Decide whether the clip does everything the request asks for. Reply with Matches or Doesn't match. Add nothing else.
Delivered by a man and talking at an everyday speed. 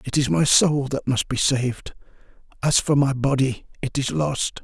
Matches